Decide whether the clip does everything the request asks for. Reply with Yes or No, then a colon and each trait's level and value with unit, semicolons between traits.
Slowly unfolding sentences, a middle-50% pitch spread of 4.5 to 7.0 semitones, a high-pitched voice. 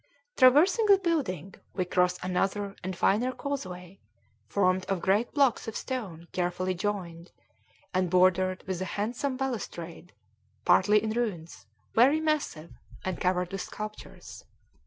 Yes: slow, 130 wpm; average, 5.1 semitones; high, 195 Hz